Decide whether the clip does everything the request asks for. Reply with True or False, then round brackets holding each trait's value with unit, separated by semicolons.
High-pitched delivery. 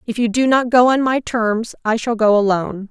True (230 Hz)